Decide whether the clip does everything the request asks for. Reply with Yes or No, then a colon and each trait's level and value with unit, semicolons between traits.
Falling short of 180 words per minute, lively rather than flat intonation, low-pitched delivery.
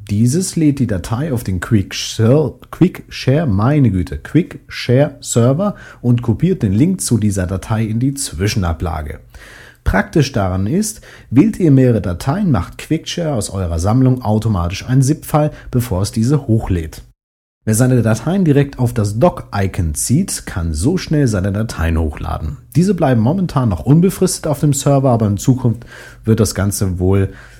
Yes: average, 155 wpm; wide, 6.2 semitones; low, 120 Hz